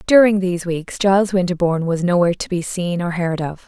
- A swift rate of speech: Yes, fast, 210 wpm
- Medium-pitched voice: Yes, medium, 180 Hz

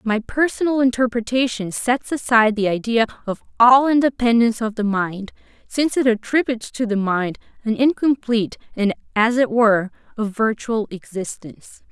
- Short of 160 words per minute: Yes, average, 140 wpm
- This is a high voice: Yes, high, 230 Hz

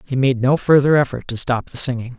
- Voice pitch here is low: Yes, low, 130 Hz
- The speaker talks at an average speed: No, fast, 250 wpm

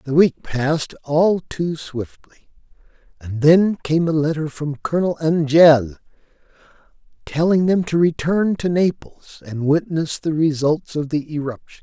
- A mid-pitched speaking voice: Yes, medium, 155 Hz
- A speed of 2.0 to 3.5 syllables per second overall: No, 4.4 syllables/s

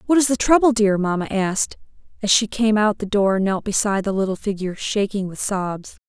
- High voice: Yes, high, 205 Hz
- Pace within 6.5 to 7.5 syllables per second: No, 5.7 syllables/s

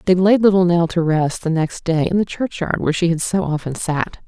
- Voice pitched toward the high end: No, medium, 170 Hz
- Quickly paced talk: Yes, fast, 250 wpm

